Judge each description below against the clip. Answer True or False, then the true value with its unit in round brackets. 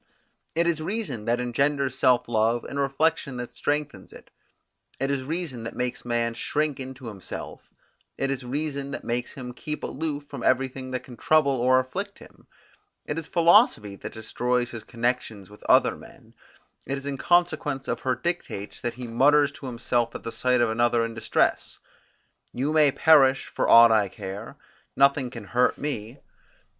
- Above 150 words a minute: True (170 wpm)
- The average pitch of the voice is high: False (130 Hz)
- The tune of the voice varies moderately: True (3.5 semitones)